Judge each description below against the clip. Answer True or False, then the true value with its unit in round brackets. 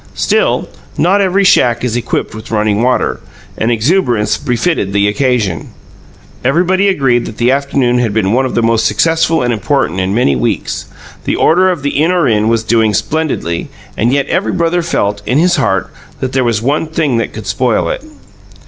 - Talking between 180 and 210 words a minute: True (185 wpm)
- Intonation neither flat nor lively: False (6.5 semitones)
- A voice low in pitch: True (125 Hz)